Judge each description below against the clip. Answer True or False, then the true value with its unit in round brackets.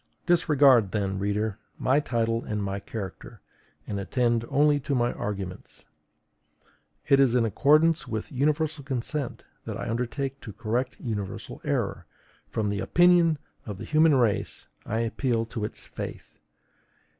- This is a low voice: True (120 Hz)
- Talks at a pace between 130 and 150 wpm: True (140 wpm)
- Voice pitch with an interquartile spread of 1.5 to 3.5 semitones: False (5.0 semitones)